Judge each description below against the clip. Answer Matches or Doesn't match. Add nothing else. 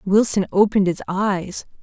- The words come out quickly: Doesn't match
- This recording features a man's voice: Doesn't match